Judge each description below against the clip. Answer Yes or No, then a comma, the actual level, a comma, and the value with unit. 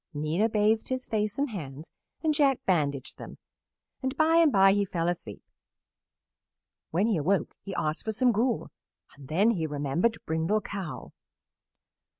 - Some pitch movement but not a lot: No, wide, 6.3 semitones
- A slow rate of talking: No, average, 150 wpm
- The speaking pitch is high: Yes, high, 200 Hz